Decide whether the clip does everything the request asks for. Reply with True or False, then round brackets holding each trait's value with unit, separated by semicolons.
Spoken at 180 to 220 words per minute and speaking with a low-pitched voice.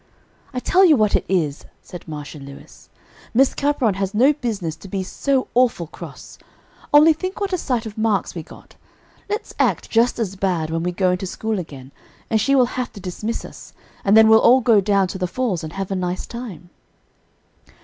False (200 wpm; 205 Hz)